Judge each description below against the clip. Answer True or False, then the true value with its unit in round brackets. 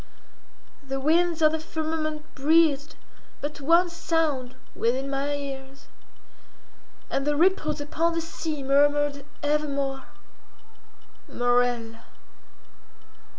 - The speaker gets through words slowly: True (90 wpm)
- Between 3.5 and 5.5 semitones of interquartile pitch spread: False (2.7 semitones)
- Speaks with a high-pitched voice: True (290 Hz)